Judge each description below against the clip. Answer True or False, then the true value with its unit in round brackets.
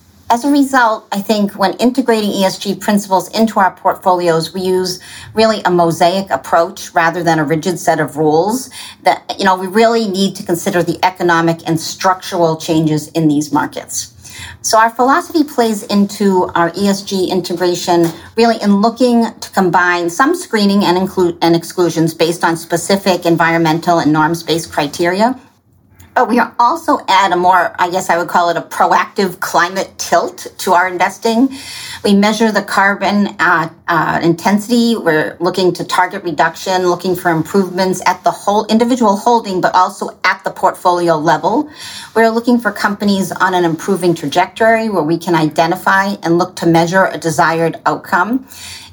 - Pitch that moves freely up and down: False (3.5 semitones)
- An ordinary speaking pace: True (165 wpm)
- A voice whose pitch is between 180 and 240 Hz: True (185 Hz)